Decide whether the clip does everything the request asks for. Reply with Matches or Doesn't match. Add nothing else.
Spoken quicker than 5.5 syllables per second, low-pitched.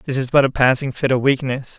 Matches